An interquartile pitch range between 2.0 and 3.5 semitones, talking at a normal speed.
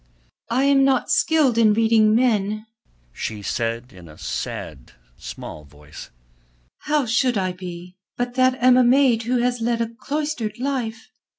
No: wide, 5.6 semitones; average, 155 wpm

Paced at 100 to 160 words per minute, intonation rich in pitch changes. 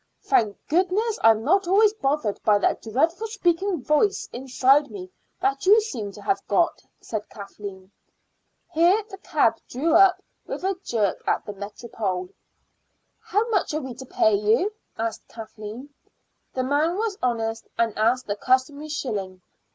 Yes: average, 150 wpm; wide, 8.4 semitones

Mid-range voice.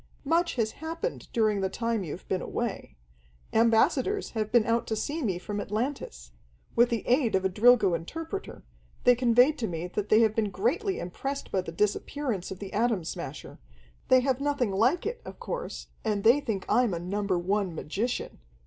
No: high, 225 Hz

